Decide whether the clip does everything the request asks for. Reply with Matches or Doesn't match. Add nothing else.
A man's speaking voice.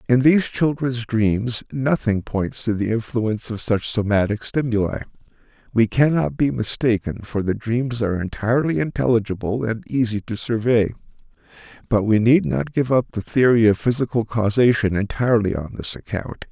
Matches